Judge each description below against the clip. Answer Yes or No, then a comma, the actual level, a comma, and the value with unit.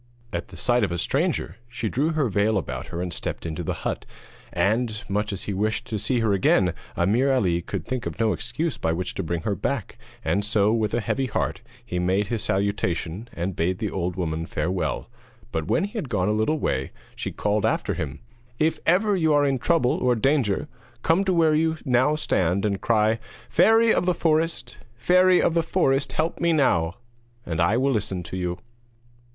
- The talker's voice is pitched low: Yes, low, 110 Hz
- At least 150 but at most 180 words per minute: No, fast, 205 wpm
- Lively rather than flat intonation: Yes, wide, 7.3 semitones